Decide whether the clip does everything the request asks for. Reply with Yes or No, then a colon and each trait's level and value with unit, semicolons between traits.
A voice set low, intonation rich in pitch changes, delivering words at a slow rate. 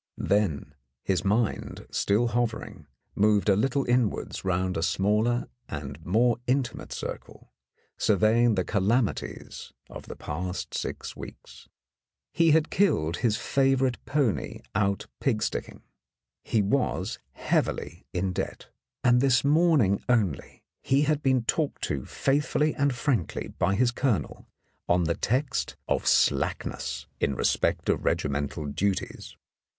Yes: low, 110 Hz; wide, 5.9 semitones; slow, 125 wpm